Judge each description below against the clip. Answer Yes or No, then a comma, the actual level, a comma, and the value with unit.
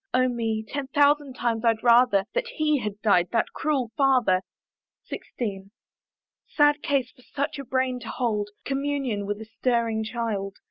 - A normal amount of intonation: Yes, average, 4.0 semitones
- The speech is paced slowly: No, average, 155 wpm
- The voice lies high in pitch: Yes, high, 240 Hz